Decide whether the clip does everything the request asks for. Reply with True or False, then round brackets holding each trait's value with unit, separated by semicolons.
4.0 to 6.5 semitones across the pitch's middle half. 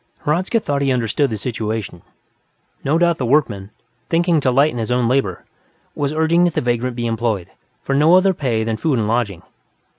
True (5.3 semitones)